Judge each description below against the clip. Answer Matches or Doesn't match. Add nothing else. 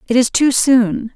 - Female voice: Matches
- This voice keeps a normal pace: Doesn't match